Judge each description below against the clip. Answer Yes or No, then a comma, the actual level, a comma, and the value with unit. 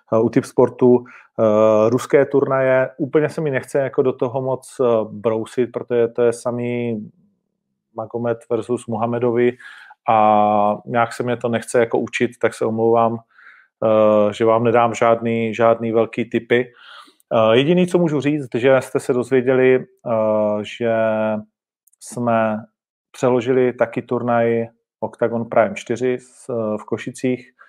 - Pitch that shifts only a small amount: Yes, narrow, 2.1 semitones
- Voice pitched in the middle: No, low, 120 Hz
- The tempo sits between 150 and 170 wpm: No, average, 130 wpm